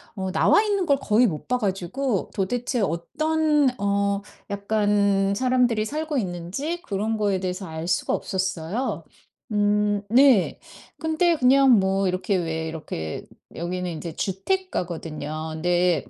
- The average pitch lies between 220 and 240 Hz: No, high, 200 Hz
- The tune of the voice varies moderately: No, wide, 5.8 semitones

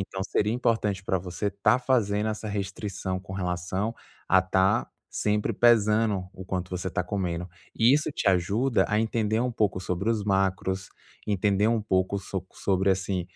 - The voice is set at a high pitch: No, low, 100 Hz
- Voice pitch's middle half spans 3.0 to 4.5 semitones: No, narrow, 2.5 semitones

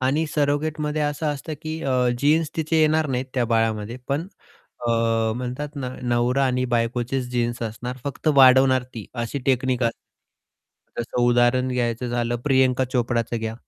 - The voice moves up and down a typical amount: Yes, average, 3.1 semitones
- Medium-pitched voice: No, low, 130 Hz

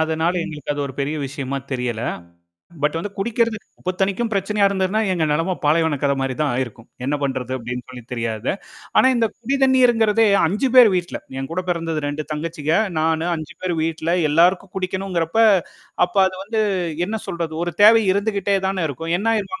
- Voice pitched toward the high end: No, medium, 170 Hz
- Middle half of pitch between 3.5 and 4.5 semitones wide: No, wide, 5.4 semitones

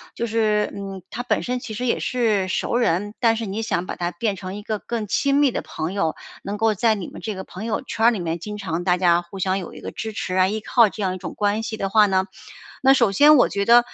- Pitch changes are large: No, average, 3.3 semitones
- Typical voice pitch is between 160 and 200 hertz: No, high, 210 Hz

